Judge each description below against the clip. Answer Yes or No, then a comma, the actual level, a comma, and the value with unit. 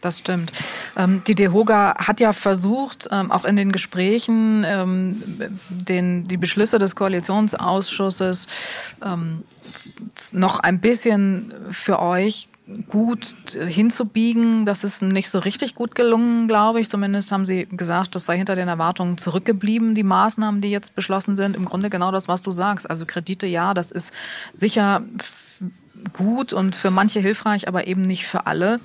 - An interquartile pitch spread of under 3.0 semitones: Yes, narrow, 2.6 semitones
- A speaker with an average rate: Yes, average, 145 wpm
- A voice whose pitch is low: No, high, 195 Hz